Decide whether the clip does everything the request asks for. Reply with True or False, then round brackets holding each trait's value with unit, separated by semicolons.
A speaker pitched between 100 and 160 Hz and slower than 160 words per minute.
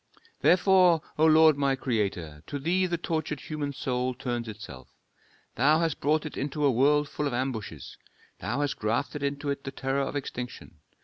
False (140 Hz; 175 wpm)